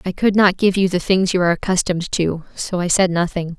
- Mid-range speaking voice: Yes, medium, 180 Hz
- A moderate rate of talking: No, fast, 250 wpm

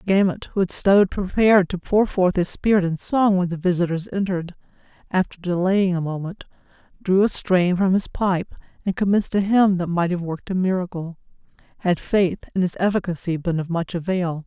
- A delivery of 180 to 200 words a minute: Yes, average, 185 wpm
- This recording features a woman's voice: Yes, female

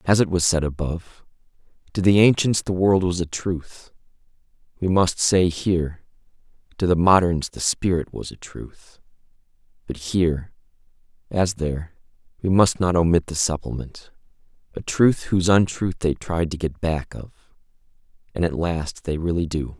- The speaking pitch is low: Yes, very low, 85 Hz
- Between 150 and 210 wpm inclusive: Yes, average, 155 wpm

